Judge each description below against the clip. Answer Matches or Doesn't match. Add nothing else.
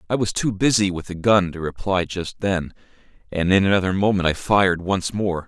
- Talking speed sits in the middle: Doesn't match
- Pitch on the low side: Matches